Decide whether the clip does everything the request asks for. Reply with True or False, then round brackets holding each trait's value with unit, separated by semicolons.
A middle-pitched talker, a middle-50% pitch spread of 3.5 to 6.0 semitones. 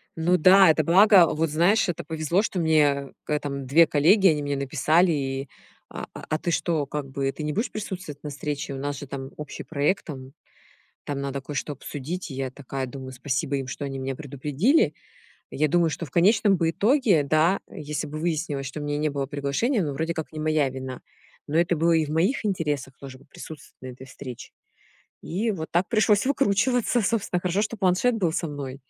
True (155 Hz; 4.2 semitones)